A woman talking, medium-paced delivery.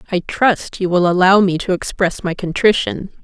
Yes: female; average, 185 wpm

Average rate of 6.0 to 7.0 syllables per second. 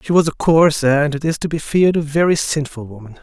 Yes: 6.1 syllables/s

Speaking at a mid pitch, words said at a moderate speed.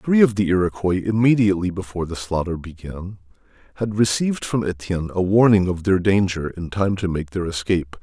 No: very low, 95 Hz; average, 180 wpm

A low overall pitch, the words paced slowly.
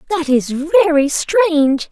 No: very high, 315 Hz; slow, 125 wpm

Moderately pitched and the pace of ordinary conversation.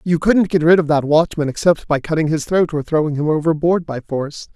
No: medium, 160 Hz; fast, 235 wpm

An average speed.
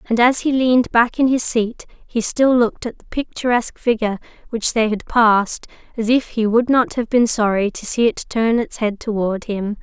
No: fast, 215 wpm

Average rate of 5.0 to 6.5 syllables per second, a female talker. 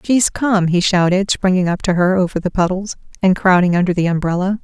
Yes: 5.6 syllables/s; female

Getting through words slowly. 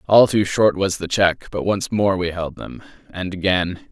No: average, 200 wpm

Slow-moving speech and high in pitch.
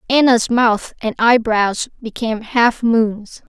Yes: slow, 120 wpm; high, 230 Hz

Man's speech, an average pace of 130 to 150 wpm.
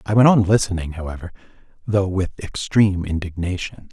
Yes: male; average, 140 wpm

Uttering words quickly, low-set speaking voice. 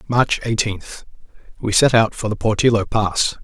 No: average, 140 wpm; low, 110 Hz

